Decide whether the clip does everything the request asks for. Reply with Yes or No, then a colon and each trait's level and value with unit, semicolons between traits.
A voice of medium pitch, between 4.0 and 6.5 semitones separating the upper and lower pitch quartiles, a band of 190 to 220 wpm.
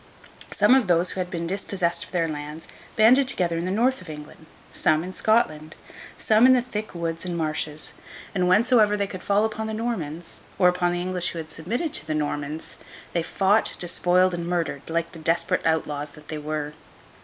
Yes: medium, 175 Hz; average, 4.4 semitones; average, 200 wpm